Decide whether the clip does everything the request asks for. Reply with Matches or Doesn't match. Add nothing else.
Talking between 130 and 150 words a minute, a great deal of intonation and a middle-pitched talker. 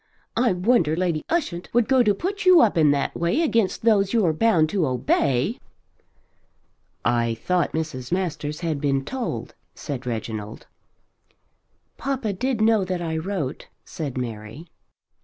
Matches